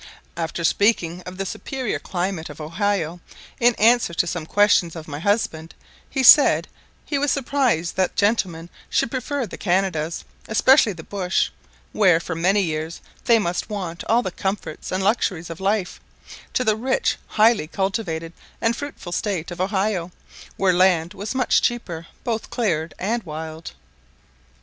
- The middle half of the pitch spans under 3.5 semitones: No, average, 4.7 semitones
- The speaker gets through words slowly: No, average, 155 wpm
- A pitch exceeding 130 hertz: Yes, high, 190 Hz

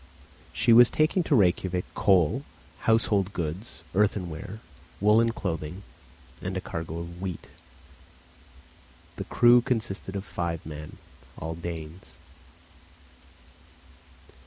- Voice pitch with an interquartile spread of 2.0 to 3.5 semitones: No, average, 4.5 semitones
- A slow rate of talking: Yes, slow, 100 wpm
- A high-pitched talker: No, very low, 95 Hz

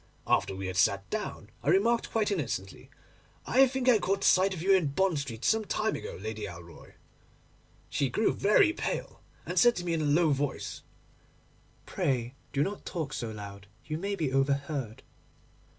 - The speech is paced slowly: No, average, 175 wpm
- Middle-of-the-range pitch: Yes, medium, 150 Hz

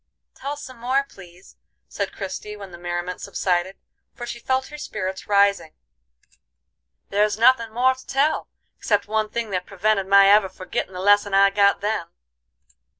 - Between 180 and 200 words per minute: No, average, 155 wpm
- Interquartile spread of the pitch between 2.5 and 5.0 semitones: Yes, average, 3.6 semitones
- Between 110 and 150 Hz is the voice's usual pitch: No, high, 205 Hz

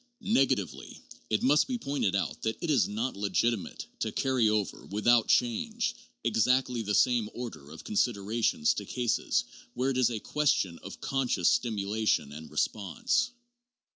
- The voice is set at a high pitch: No, low, 115 Hz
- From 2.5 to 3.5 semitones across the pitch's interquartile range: No, average, 4.0 semitones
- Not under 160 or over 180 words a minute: No, average, 145 wpm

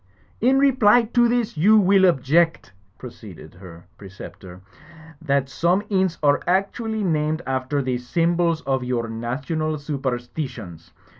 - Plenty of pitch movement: Yes, wide, 7.3 semitones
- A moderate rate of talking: No, slow, 130 wpm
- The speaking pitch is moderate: Yes, medium, 150 Hz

